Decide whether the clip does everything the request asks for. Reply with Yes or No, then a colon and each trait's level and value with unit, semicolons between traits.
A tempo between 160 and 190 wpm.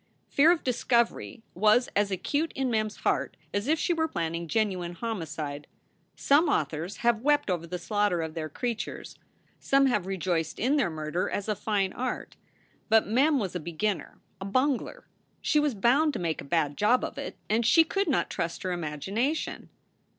Yes: average, 180 wpm